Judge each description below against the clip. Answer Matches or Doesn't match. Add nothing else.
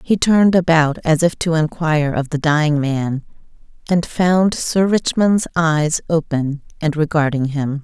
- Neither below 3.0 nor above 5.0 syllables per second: Matches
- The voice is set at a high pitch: Doesn't match